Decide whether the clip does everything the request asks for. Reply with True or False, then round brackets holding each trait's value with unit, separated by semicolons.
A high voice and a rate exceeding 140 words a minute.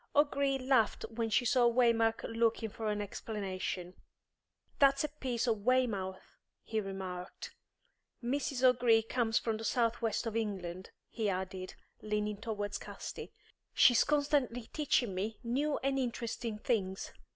False (225 Hz; 135 wpm)